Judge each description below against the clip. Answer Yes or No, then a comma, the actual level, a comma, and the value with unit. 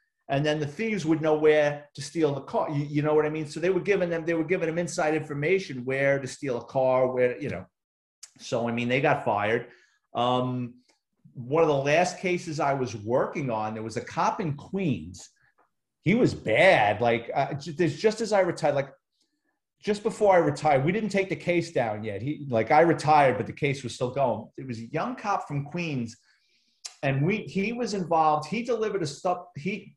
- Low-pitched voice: No, medium, 155 Hz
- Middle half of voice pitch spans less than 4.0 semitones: No, average, 5.1 semitones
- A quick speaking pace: Yes, fast, 215 wpm